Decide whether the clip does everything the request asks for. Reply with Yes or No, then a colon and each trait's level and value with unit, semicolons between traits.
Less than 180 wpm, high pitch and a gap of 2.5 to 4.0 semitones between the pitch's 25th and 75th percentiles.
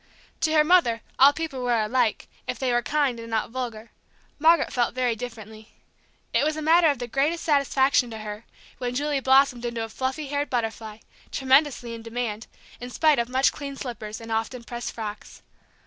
No: average, 185 wpm; very high, 250 Hz; average, 3.7 semitones